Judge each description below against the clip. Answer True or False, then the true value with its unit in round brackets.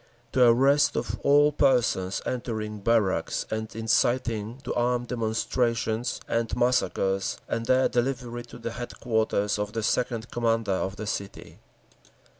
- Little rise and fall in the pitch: True (2.2 semitones)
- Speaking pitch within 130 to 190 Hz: False (115 Hz)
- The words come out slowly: True (130 wpm)